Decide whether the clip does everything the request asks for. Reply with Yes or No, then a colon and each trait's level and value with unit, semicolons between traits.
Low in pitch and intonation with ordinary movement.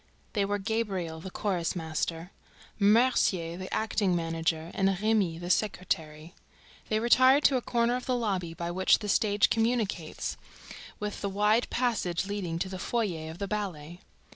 No: high, 195 Hz; average, 4.2 semitones